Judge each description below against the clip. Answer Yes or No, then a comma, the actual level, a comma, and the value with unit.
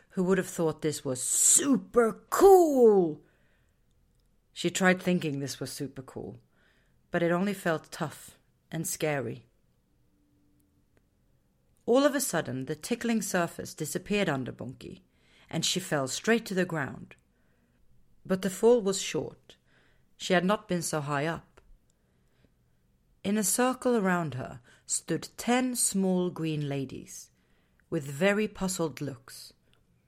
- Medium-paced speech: No, slow, 130 wpm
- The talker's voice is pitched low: No, medium, 165 Hz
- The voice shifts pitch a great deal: Yes, wide, 7.0 semitones